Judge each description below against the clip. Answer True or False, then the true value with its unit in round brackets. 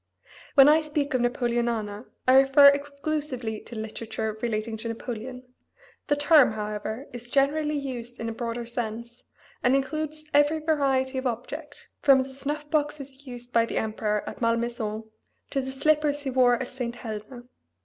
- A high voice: True (255 Hz)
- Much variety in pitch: False (3.6 semitones)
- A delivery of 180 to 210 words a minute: False (160 wpm)